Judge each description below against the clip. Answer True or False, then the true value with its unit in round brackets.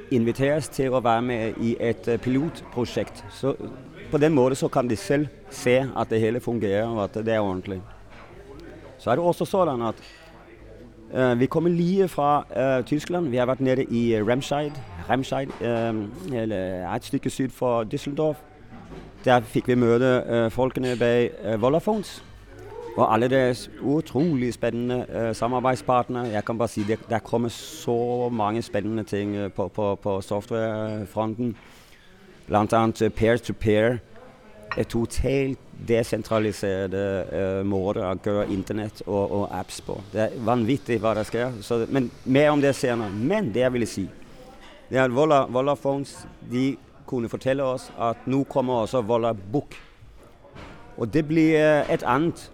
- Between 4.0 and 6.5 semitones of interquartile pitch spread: False (3.4 semitones)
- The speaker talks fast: False (160 wpm)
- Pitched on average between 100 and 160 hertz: True (120 Hz)